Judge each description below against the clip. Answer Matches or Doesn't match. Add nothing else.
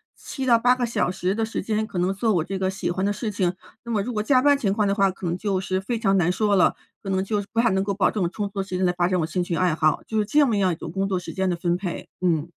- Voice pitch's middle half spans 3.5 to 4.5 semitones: Doesn't match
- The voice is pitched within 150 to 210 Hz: Matches